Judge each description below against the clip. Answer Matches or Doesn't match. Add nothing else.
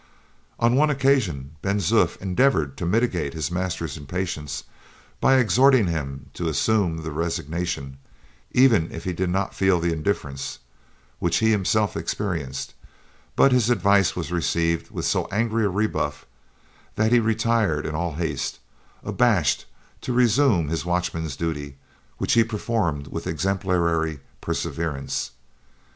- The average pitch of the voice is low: Matches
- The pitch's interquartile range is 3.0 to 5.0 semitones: Doesn't match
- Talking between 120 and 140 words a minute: Matches